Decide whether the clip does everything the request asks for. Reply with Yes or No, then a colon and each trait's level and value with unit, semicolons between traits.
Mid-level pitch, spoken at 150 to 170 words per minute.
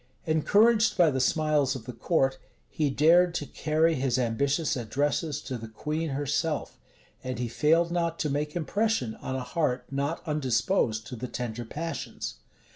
Yes: medium, 145 Hz; average, 160 wpm